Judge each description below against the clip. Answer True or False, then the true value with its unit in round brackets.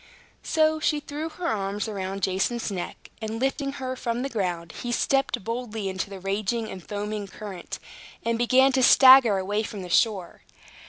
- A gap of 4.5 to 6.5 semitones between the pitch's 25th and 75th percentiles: True (4.9 semitones)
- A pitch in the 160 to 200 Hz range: False (220 Hz)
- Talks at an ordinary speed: True (170 wpm)